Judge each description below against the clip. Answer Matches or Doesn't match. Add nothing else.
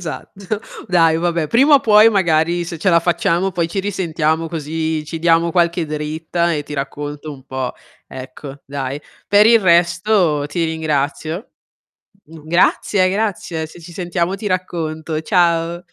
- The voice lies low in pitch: Doesn't match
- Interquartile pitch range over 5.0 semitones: Doesn't match